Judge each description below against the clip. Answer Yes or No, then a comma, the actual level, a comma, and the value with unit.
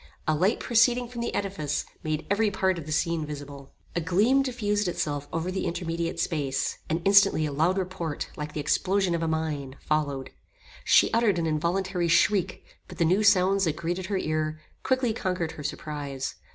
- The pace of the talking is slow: No, average, 180 wpm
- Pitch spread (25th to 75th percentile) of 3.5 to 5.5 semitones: Yes, average, 4.2 semitones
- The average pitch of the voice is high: No, medium, 170 Hz